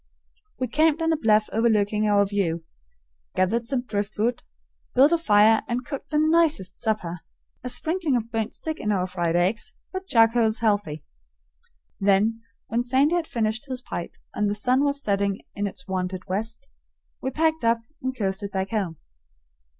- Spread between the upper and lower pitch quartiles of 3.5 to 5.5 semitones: Yes, average, 4.5 semitones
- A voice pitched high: Yes, high, 225 Hz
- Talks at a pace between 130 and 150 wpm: No, average, 165 wpm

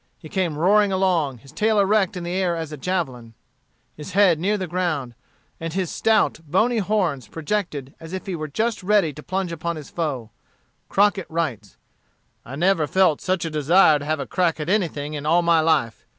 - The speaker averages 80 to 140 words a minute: No, average, 195 wpm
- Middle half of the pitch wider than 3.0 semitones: Yes, average, 4.1 semitones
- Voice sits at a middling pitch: Yes, medium, 170 Hz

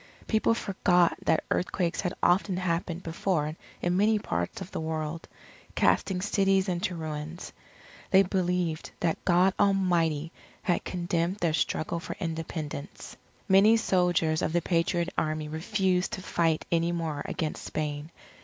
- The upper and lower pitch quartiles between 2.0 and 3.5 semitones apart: Yes, average, 2.8 semitones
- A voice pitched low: No, medium, 175 Hz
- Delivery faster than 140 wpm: No, slow, 135 wpm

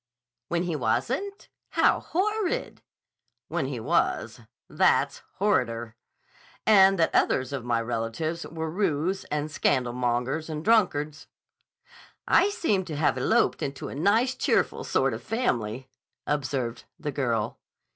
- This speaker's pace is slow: Yes, slow, 125 wpm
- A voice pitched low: No, medium, 150 Hz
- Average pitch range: No, wide, 7.4 semitones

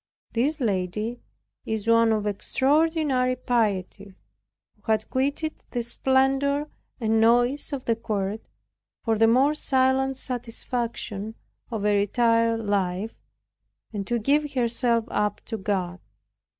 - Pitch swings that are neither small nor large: Yes, average, 3.8 semitones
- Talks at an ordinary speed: No, slow, 120 wpm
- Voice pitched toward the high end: Yes, high, 230 Hz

